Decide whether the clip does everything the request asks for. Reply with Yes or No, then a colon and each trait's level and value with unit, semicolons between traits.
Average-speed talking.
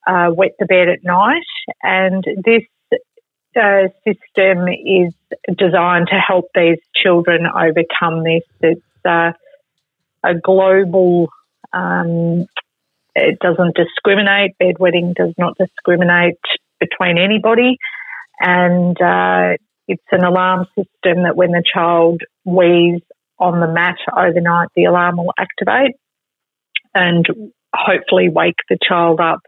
No: slow, 115 wpm